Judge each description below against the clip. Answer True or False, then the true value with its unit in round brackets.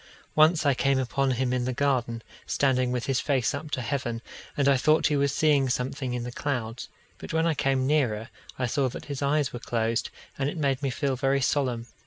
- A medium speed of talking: False (220 wpm)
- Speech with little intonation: True (2.3 semitones)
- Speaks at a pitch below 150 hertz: True (135 Hz)